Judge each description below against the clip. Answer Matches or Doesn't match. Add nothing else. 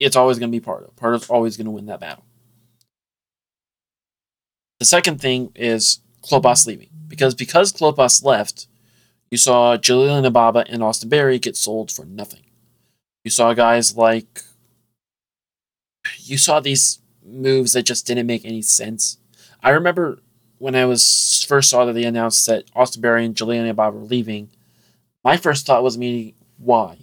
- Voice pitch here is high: Doesn't match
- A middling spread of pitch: Doesn't match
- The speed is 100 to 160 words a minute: Doesn't match